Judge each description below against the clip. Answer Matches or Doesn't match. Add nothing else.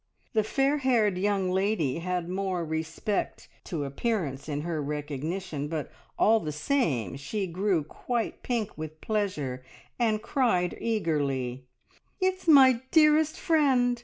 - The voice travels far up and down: Matches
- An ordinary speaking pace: Doesn't match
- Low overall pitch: Doesn't match